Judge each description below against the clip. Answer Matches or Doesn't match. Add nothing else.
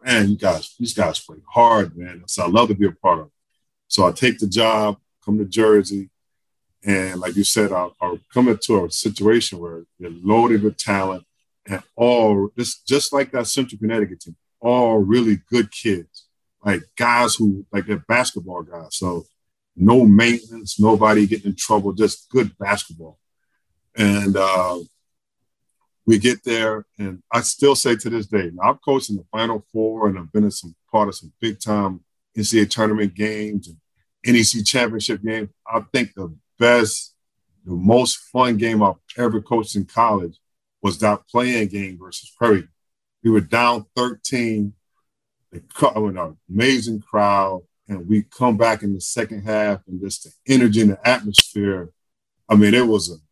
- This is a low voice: Matches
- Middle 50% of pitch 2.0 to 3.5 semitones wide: Matches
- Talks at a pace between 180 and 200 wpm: Doesn't match